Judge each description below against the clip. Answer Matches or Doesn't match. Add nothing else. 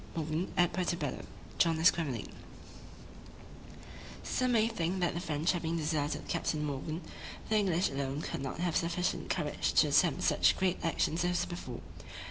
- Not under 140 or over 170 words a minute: Matches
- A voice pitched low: Doesn't match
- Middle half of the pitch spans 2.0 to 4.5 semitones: Matches